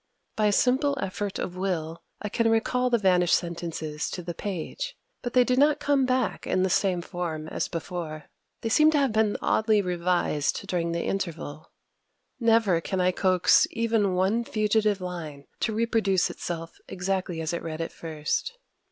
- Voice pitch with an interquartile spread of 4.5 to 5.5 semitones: Yes, average, 4.9 semitones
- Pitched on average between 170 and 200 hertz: Yes, high, 190 Hz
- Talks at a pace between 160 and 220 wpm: Yes, average, 170 wpm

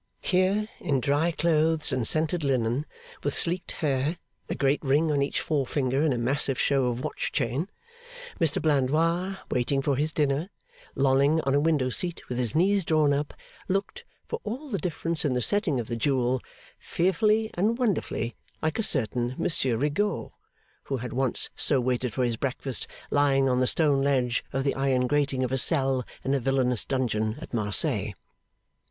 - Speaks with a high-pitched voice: No, medium, 140 Hz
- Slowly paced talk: No, average, 175 wpm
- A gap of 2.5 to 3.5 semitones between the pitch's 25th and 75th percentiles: No, average, 4.0 semitones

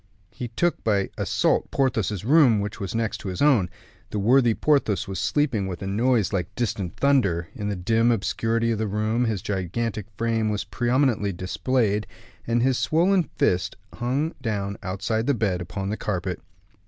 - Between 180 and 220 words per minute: No, average, 170 wpm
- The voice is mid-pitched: No, low, 110 Hz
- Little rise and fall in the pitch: No, average, 3.7 semitones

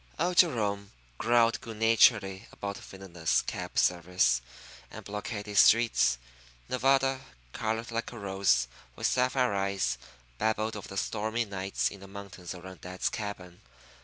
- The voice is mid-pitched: No, low, 100 Hz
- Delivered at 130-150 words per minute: Yes, slow, 135 wpm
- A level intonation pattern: No, average, 3.3 semitones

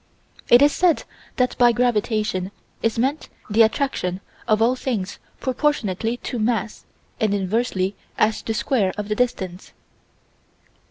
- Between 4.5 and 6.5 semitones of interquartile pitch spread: No, average, 3.4 semitones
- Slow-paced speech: Yes, slow, 130 wpm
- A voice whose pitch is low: No, high, 225 Hz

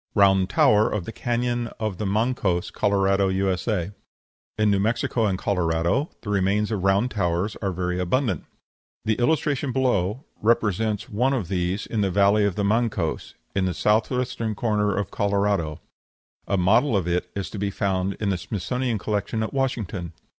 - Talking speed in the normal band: Yes, average, 170 wpm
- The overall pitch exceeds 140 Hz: No, low, 100 Hz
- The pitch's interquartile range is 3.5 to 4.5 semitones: No, average, 3.0 semitones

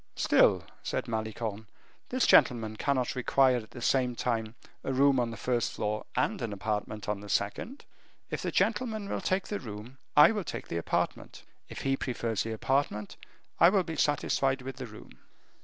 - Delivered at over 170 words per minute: Yes, average, 180 wpm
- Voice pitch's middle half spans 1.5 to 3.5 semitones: No, average, 4.0 semitones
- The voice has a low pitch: Yes, low, 125 Hz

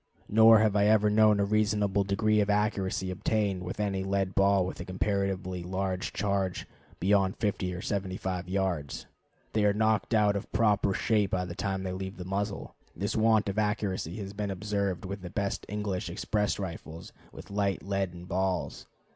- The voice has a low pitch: Yes, low, 100 Hz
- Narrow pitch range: Yes, narrow, 1.8 semitones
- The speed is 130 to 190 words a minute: Yes, average, 175 wpm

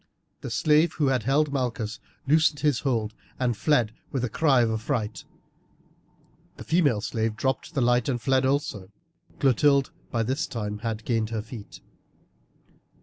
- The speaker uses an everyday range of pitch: Yes, average, 4.2 semitones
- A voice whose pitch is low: Yes, low, 125 Hz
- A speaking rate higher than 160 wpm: No, average, 145 wpm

